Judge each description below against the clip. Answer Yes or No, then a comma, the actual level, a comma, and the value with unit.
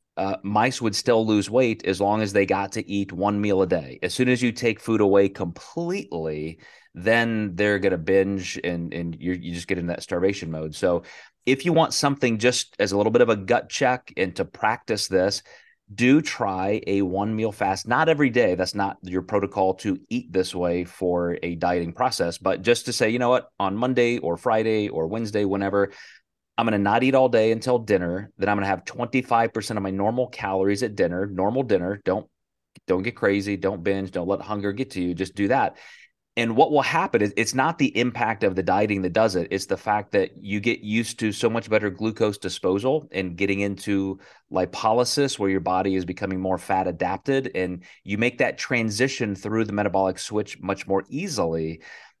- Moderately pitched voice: No, low, 100 Hz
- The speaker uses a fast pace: Yes, fast, 210 wpm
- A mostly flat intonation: No, average, 3.6 semitones